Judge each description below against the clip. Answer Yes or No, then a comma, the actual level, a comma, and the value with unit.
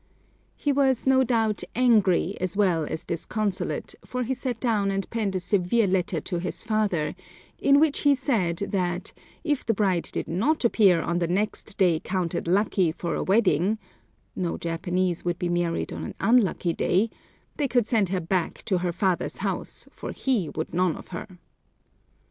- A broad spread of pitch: No, average, 4.5 semitones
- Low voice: No, high, 195 Hz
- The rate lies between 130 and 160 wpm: No, average, 175 wpm